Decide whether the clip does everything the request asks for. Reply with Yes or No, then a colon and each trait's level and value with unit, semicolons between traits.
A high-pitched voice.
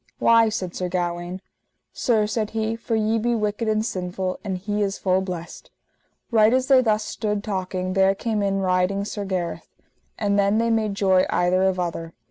Yes: high, 200 Hz